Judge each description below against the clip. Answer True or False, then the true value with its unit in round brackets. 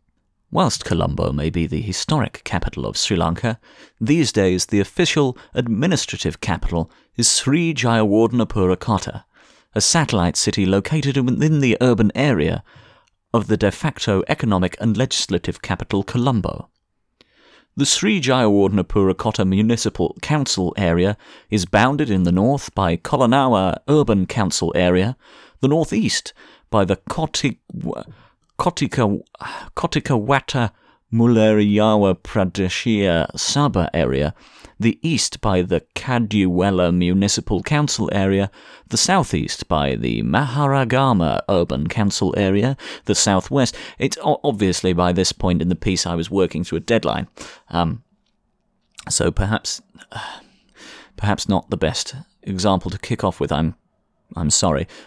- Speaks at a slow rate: True (120 wpm)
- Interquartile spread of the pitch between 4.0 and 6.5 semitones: True (4.8 semitones)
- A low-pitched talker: True (100 Hz)